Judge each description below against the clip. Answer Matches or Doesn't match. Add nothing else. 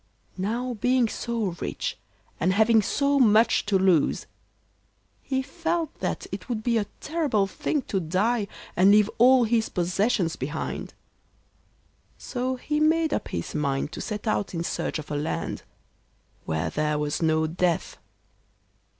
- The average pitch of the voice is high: Matches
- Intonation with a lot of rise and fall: Matches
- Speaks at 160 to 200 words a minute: Doesn't match